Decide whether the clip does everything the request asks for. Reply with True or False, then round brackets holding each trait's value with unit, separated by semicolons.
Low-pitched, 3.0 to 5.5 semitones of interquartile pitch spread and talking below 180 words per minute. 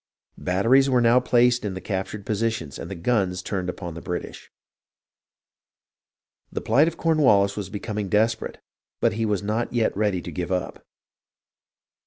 True (105 Hz; 4.0 semitones; 155 wpm)